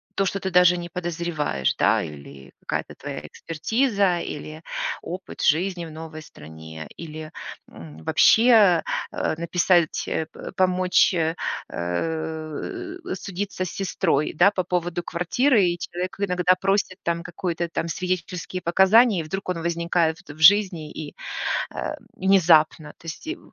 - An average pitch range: Yes, average, 3.0 semitones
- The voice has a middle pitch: Yes, medium, 175 Hz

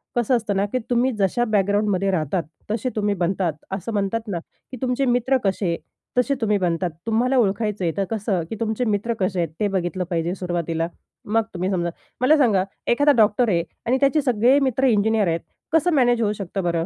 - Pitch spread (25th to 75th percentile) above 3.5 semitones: Yes, average, 4.5 semitones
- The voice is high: Yes, high, 210 Hz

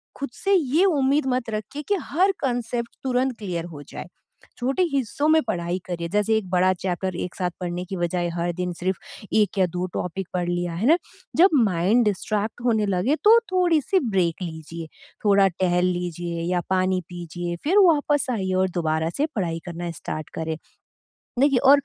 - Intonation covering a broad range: Yes, wide, 6.9 semitones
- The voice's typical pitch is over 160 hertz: Yes, high, 190 Hz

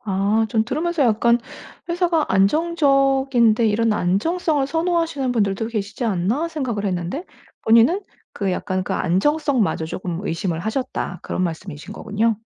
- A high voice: Yes, high, 230 Hz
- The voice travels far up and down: Yes, wide, 6.6 semitones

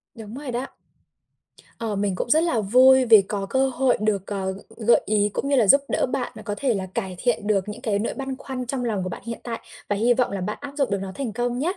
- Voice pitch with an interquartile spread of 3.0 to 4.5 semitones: Yes, average, 4.1 semitones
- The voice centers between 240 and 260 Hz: No, high, 230 Hz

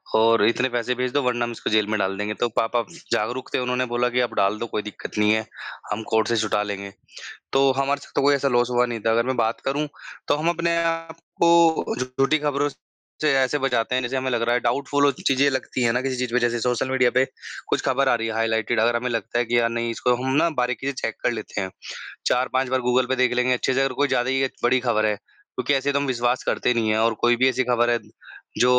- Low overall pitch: Yes, low, 125 Hz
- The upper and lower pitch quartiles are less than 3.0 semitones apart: Yes, narrow, 2.4 semitones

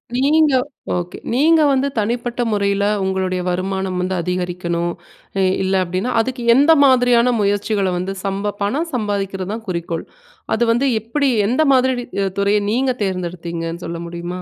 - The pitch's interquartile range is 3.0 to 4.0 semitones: No, average, 5.3 semitones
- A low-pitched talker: No, high, 200 Hz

